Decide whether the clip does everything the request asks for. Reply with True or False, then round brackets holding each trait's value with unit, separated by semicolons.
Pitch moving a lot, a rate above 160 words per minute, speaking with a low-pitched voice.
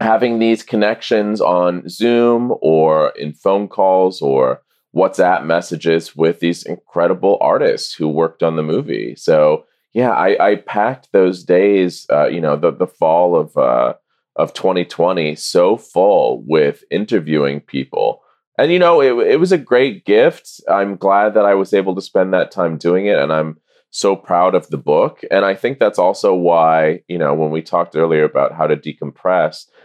True (6.0 semitones; 175 wpm; 95 Hz)